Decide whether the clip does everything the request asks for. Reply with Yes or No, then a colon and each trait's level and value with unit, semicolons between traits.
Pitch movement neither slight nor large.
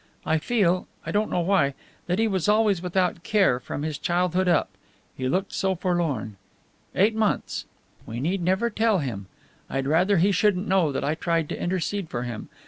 Yes: average, 4.2 semitones